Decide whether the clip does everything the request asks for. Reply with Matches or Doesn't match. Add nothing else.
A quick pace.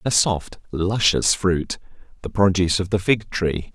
Doesn't match